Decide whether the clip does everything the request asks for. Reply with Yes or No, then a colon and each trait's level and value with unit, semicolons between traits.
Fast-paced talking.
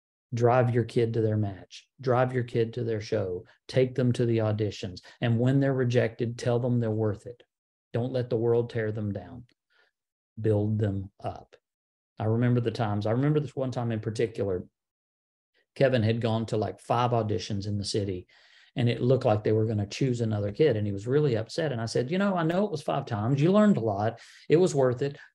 Yes: fast, 220 wpm